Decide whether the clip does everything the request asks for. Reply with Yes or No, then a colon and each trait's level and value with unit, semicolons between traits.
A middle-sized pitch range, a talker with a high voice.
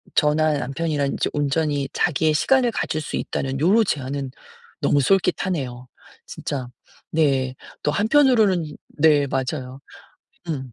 No: average, 3.4 semitones; medium, 150 Hz